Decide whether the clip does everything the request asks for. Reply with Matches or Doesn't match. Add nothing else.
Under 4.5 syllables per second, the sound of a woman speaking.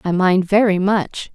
Matches